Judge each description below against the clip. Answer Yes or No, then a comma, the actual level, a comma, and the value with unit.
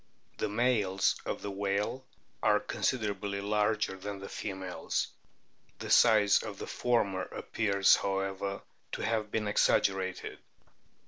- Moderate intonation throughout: No, narrow, 1.6 semitones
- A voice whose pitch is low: Yes, low, 100 Hz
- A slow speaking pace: Yes, slow, 125 wpm